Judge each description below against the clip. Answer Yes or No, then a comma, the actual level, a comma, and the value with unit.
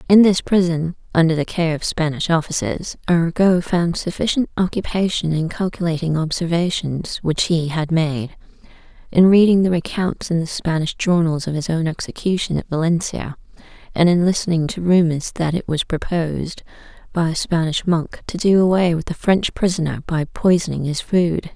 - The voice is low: No, medium, 170 Hz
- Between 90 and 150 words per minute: No, average, 160 wpm